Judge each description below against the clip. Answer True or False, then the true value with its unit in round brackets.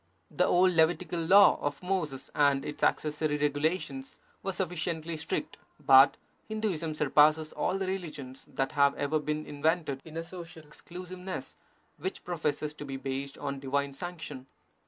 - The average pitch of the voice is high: False (155 Hz)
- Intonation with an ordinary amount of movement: True (3.8 semitones)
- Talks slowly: False (145 wpm)